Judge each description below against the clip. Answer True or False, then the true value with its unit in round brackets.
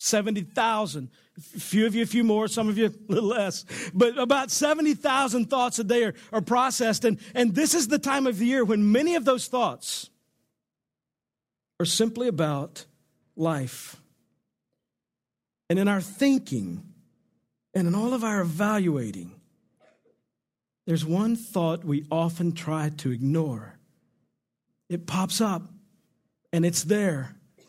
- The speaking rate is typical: True (145 wpm)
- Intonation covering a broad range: True (6.4 semitones)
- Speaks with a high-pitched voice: True (210 Hz)